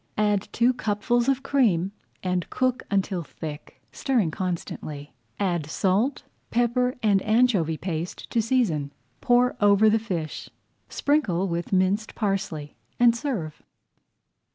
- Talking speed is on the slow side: Yes, slow, 120 wpm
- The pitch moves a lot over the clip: Yes, wide, 5.7 semitones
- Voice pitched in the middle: No, high, 205 Hz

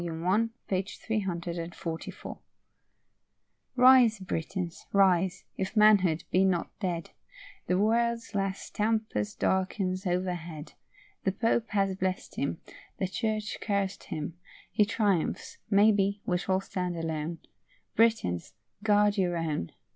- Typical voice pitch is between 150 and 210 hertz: Yes, high, 190 Hz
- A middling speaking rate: No, slow, 110 wpm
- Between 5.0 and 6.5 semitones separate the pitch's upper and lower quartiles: No, average, 3.2 semitones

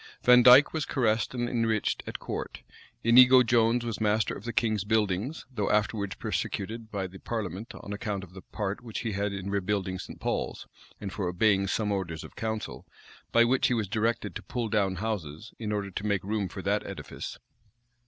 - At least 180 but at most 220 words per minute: Yes, average, 190 wpm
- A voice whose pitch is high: No, low, 105 Hz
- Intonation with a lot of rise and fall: No, average, 2.8 semitones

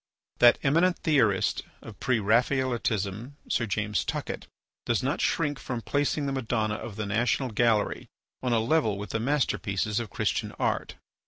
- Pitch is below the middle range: Yes, low, 120 Hz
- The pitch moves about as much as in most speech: Yes, average, 4.1 semitones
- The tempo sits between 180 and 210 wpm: No, average, 155 wpm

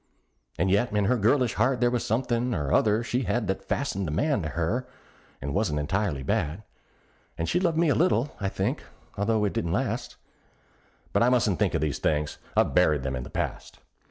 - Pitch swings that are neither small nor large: No, wide, 7.1 semitones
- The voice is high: No, low, 105 Hz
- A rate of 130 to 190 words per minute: No, fast, 205 wpm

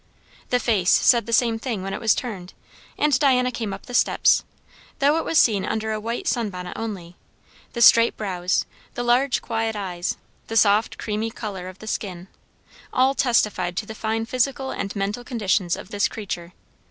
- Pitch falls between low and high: No, high, 220 Hz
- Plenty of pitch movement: No, average, 3.7 semitones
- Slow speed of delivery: No, average, 185 wpm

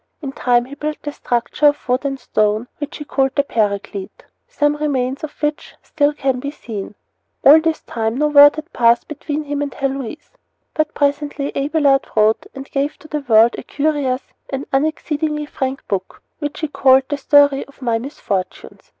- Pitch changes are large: No, average, 3.0 semitones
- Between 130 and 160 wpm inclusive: No, average, 180 wpm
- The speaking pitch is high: Yes, very high, 280 Hz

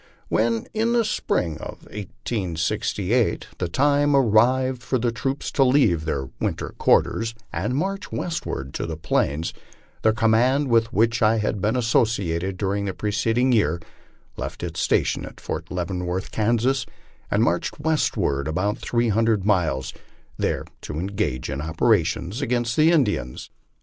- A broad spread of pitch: Yes, wide, 5.7 semitones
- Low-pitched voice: Yes, low, 110 Hz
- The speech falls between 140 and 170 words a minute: Yes, average, 150 wpm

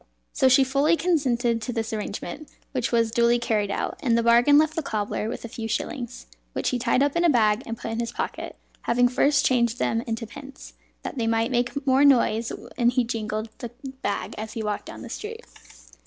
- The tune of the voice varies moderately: Yes, average, 3.3 semitones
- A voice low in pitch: No, high, 240 Hz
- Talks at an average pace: No, fast, 215 wpm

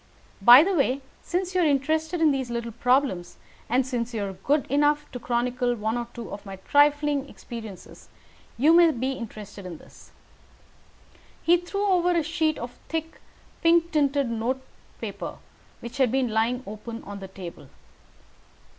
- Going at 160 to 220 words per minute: Yes, average, 165 wpm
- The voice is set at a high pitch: Yes, very high, 260 Hz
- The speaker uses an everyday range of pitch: Yes, average, 5.0 semitones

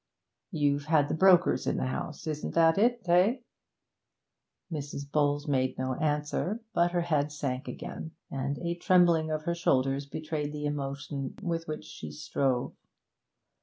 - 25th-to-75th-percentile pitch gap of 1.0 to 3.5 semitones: Yes, average, 3.2 semitones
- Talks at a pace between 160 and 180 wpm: No, average, 150 wpm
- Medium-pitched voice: Yes, medium, 150 Hz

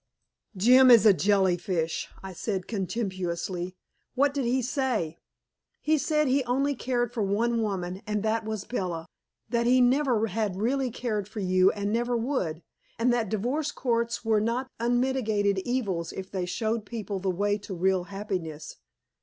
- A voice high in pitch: Yes, high, 215 Hz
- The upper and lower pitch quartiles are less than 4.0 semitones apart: No, average, 4.4 semitones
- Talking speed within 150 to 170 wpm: Yes, average, 160 wpm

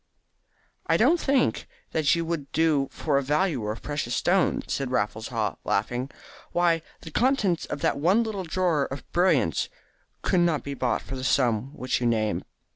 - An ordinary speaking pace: Yes, average, 175 wpm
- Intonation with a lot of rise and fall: Yes, wide, 5.7 semitones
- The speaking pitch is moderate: Yes, medium, 145 Hz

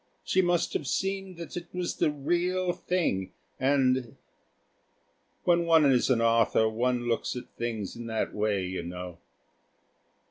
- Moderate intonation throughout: No, wide, 7.4 semitones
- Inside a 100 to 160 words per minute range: Yes, average, 145 wpm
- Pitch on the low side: Yes, low, 130 Hz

